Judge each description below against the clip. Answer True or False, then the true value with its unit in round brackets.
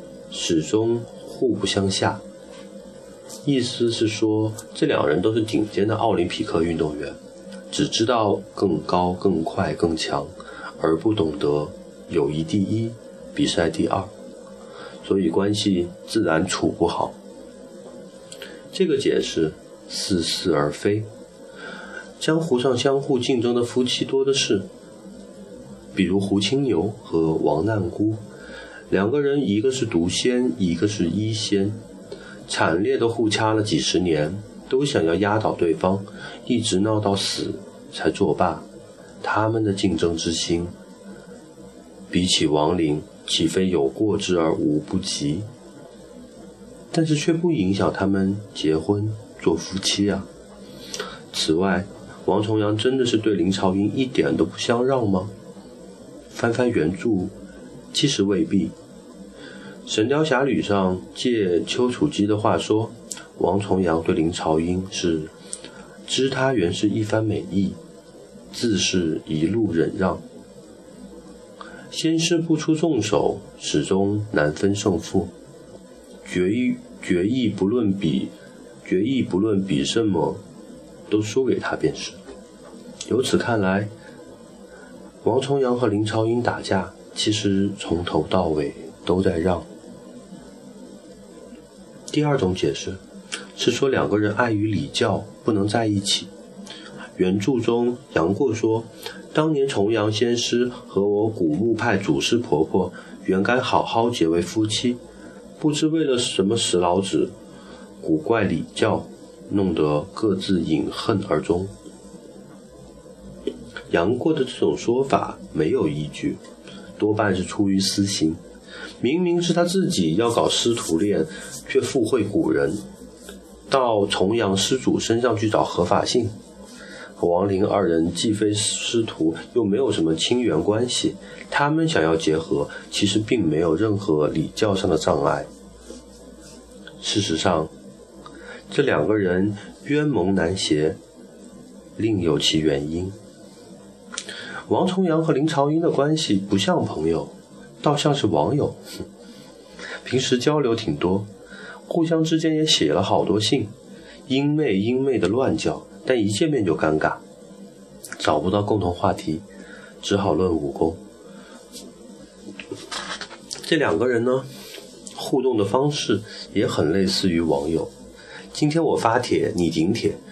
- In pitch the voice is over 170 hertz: False (105 Hz)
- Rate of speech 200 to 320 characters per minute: False (185 characters per minute)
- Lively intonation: False (4.9 semitones)